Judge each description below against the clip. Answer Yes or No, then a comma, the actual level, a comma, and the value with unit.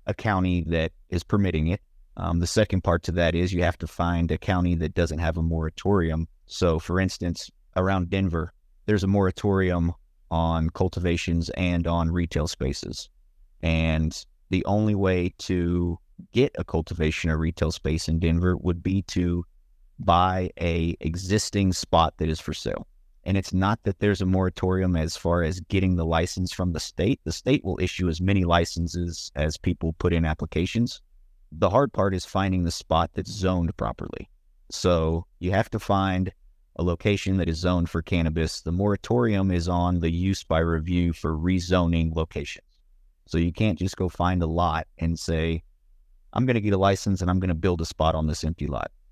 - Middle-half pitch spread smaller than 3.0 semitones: Yes, narrow, 2.4 semitones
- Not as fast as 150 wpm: No, average, 185 wpm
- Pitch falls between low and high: No, very low, 85 Hz